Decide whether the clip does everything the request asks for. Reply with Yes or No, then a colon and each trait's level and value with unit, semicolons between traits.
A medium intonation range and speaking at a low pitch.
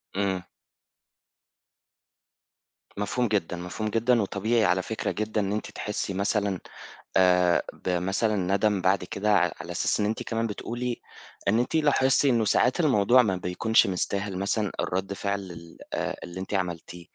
Yes: average, 3.3 semitones; low, 100 Hz